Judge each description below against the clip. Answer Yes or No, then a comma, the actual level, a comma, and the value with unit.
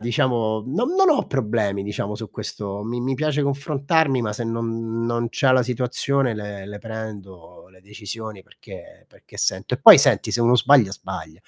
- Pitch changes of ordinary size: Yes, average, 3.9 semitones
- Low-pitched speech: Yes, low, 115 Hz